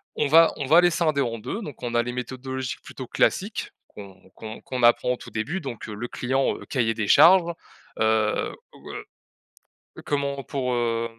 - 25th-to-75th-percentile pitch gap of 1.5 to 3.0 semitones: No, average, 3.6 semitones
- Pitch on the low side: Yes, low, 125 Hz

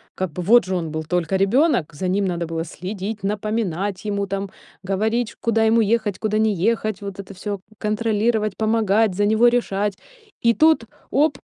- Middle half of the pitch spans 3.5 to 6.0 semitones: No, average, 2.8 semitones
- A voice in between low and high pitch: No, high, 205 Hz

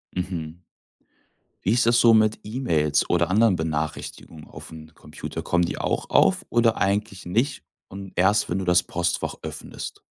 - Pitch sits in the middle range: No, very low, 95 Hz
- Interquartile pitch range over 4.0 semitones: Yes, average, 4.5 semitones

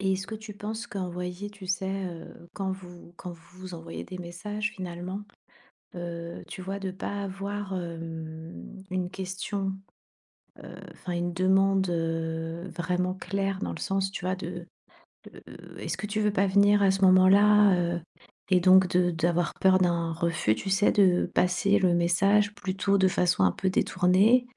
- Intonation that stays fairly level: Yes, narrow, 2.1 semitones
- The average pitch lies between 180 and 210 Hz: Yes, medium, 185 Hz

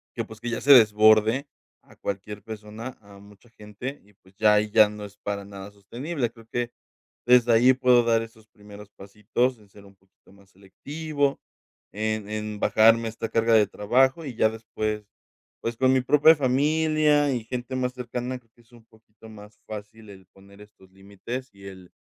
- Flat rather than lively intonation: No, average, 3.3 semitones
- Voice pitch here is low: Yes, low, 110 Hz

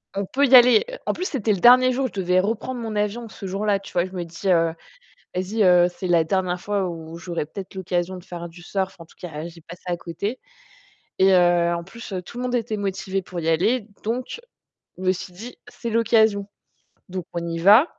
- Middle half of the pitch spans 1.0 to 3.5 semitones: No, average, 4.1 semitones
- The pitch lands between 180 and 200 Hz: Yes, high, 190 Hz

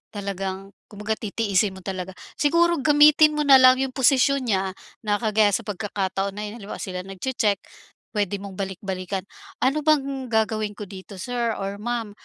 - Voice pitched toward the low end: No, high, 210 Hz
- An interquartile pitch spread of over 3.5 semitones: Yes, average, 4.9 semitones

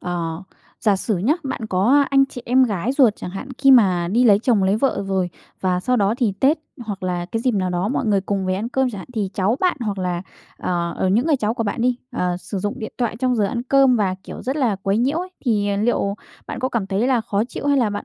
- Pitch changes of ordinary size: Yes, average, 4.7 semitones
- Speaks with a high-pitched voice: Yes, high, 215 Hz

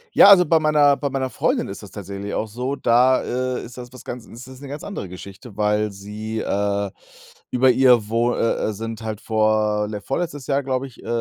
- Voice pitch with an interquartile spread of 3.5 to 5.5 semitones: Yes, average, 3.8 semitones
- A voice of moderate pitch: No, low, 120 Hz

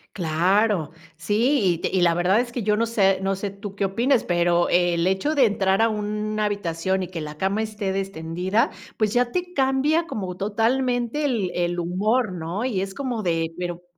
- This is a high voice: Yes, high, 200 Hz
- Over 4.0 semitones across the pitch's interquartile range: Yes, average, 4.4 semitones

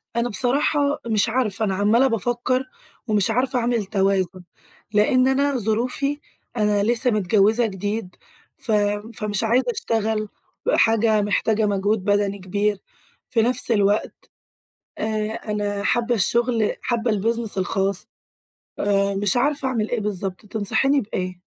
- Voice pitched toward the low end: No, high, 220 Hz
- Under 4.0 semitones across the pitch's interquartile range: Yes, average, 3.0 semitones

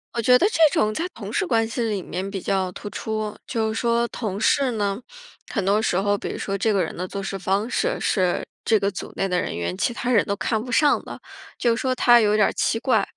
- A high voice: Yes, high, 215 Hz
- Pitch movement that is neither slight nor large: Yes, average, 3.3 semitones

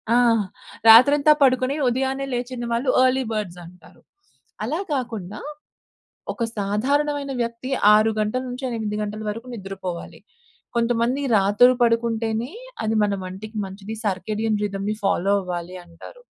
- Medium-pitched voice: No, high, 225 Hz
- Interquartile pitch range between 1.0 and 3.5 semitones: No, average, 4.1 semitones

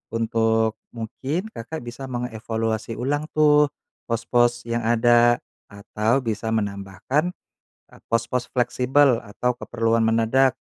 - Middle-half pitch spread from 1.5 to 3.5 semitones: Yes, narrow, 2.4 semitones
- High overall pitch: No, low, 120 Hz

